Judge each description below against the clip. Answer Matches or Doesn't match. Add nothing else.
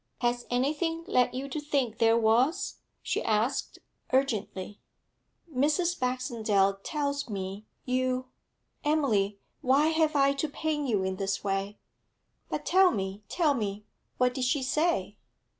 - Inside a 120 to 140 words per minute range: Matches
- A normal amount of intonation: Doesn't match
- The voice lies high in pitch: Matches